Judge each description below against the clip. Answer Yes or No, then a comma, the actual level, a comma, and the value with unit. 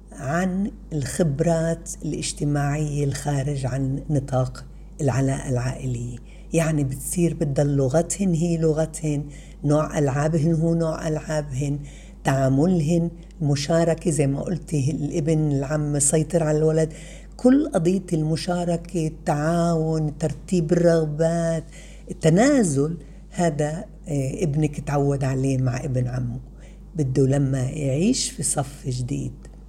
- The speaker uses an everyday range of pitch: Yes, average, 3.0 semitones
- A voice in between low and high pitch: Yes, medium, 155 Hz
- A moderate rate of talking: Yes, average, 100 wpm